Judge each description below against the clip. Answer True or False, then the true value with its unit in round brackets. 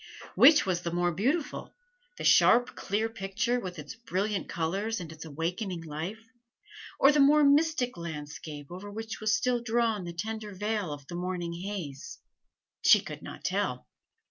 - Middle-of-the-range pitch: False (195 Hz)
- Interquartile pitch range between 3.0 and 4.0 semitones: False (4.9 semitones)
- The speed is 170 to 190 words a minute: False (160 wpm)